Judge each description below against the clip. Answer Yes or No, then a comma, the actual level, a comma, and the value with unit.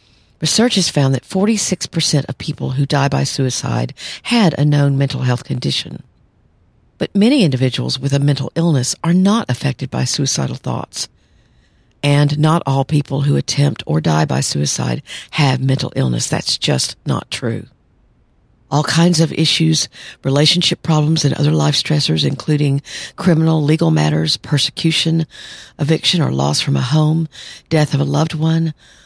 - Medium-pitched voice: Yes, medium, 145 Hz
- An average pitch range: Yes, average, 3.4 semitones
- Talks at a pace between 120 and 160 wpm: Yes, average, 150 wpm